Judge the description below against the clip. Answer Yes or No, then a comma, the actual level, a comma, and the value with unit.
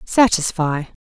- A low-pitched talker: No, medium, 180 Hz